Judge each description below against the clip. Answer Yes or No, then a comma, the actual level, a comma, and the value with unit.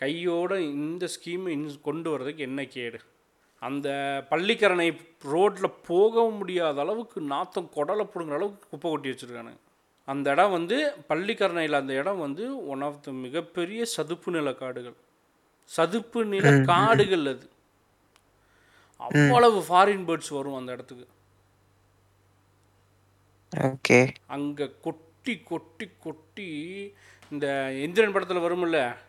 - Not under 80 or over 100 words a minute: No, average, 110 wpm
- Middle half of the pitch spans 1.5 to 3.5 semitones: No, wide, 5.4 semitones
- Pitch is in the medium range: Yes, medium, 150 Hz